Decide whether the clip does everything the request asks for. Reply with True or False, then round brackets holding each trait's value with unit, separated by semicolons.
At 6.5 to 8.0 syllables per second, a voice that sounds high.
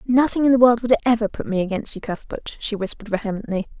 True (6.7 syllables/s; 225 Hz)